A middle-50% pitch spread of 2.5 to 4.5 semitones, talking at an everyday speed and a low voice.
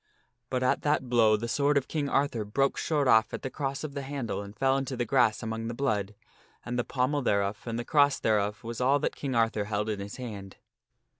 No: average, 4.2 semitones; fast, 230 wpm; low, 120 Hz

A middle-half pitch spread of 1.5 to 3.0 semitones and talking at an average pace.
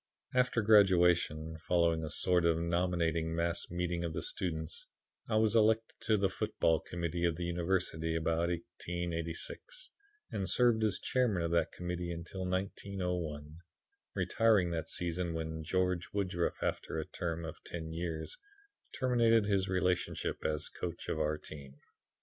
Yes: narrow, 2.5 semitones; average, 145 wpm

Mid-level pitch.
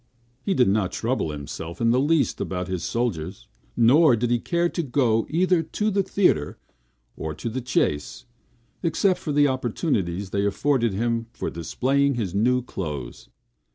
No: low, 120 Hz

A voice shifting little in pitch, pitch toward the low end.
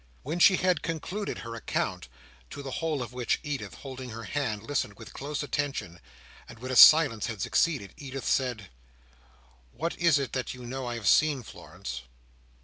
No: average, 4.2 semitones; low, 130 Hz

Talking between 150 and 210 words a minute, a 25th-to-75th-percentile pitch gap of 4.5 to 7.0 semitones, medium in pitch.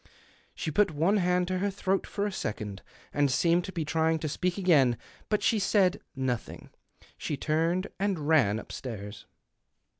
Yes: average, 160 wpm; average, 5.2 semitones; medium, 165 Hz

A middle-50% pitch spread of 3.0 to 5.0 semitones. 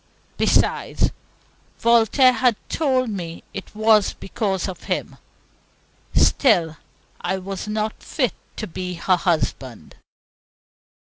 Yes: average, 4.5 semitones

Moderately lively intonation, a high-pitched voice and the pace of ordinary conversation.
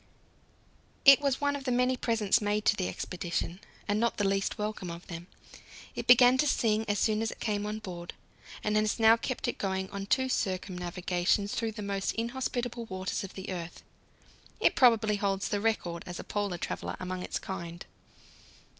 Yes: average, 3.5 semitones; high, 205 Hz; average, 185 wpm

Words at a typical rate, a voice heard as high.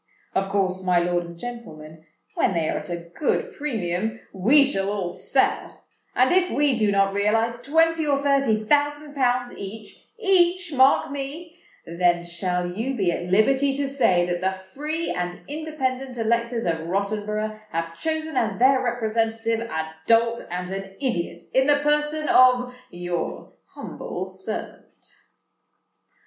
Yes: average, 145 wpm; high, 225 Hz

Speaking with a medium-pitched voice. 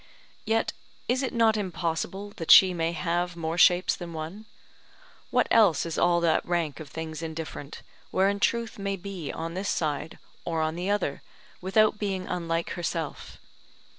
Yes: medium, 175 Hz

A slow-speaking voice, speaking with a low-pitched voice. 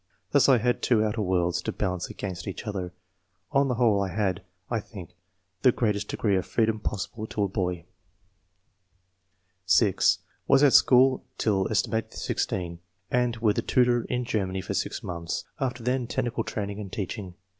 No: average, 170 wpm; low, 105 Hz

